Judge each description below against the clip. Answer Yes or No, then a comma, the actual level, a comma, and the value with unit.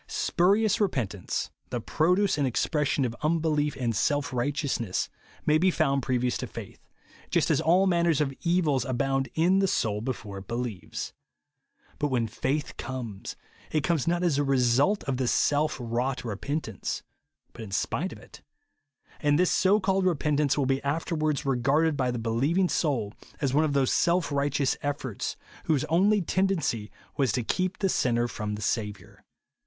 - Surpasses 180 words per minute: No, average, 170 wpm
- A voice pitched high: No, medium, 140 Hz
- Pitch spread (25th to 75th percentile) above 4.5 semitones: Yes, average, 5.1 semitones